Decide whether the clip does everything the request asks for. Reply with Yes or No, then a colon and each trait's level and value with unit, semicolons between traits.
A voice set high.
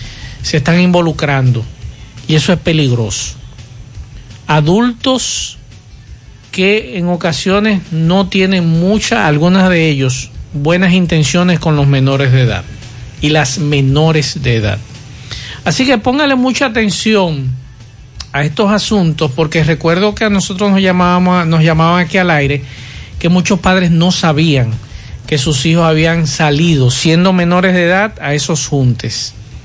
No: medium, 160 Hz